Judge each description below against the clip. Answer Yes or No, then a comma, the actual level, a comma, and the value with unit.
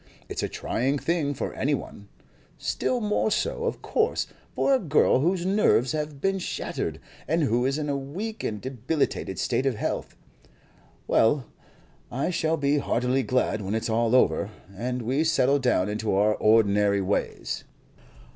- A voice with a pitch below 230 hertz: Yes, low, 135 Hz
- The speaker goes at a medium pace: Yes, average, 160 wpm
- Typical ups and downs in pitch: No, wide, 5.8 semitones